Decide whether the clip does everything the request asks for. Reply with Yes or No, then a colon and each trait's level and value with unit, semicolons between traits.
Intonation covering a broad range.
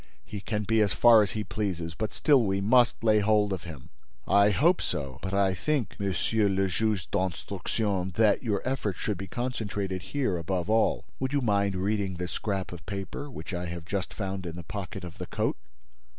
No: average, 2.9 semitones